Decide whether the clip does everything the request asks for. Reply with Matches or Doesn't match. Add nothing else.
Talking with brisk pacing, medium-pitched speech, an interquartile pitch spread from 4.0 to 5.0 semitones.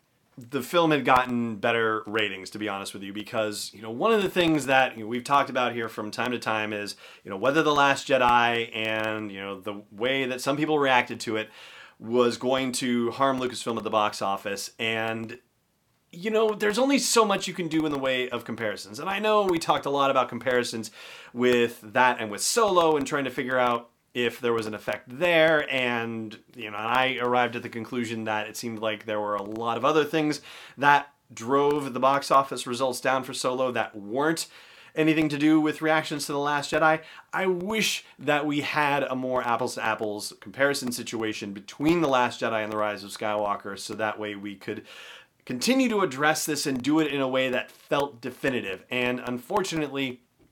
Doesn't match